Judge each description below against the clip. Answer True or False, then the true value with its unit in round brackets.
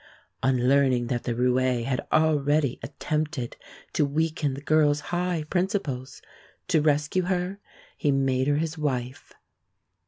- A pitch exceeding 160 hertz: False (145 Hz)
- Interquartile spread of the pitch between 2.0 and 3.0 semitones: False (3.4 semitones)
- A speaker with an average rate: False (130 wpm)